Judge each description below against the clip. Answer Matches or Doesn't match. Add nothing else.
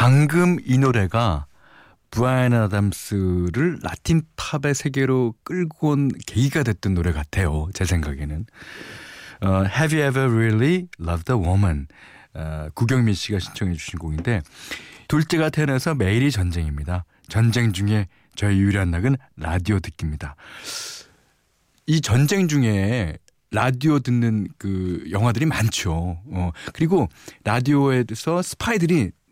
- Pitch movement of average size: Doesn't match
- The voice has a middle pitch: Doesn't match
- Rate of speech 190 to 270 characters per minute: Doesn't match